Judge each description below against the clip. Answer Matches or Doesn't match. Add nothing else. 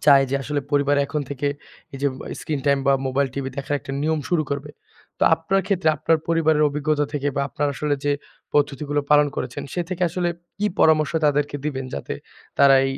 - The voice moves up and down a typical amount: Doesn't match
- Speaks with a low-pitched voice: Doesn't match